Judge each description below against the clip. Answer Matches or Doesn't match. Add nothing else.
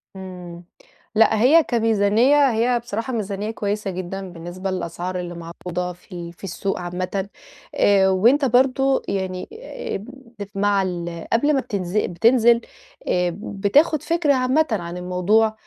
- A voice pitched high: Matches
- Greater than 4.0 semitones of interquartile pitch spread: Matches